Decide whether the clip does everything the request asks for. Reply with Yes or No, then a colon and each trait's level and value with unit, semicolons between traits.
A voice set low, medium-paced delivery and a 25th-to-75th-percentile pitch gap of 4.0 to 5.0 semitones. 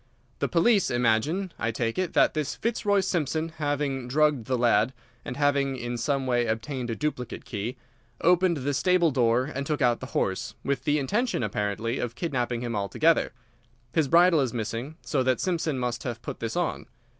Yes: low, 130 Hz; average, 180 wpm; average, 4.7 semitones